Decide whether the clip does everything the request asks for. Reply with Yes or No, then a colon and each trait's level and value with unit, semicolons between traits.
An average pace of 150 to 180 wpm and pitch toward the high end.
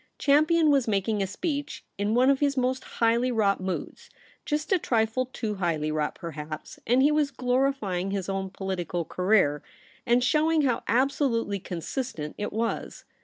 Yes: average, 170 wpm; high, 230 Hz